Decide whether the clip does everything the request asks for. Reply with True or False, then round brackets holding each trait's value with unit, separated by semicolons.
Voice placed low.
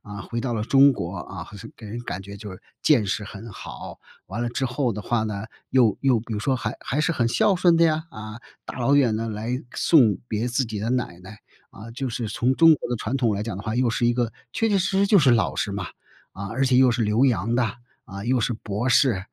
True (115 Hz)